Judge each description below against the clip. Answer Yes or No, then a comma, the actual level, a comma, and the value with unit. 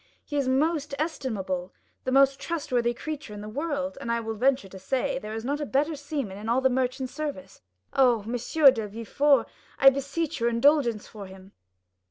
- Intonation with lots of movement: No, average, 4.1 semitones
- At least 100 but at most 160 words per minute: No, average, 195 wpm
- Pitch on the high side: Yes, very high, 260 Hz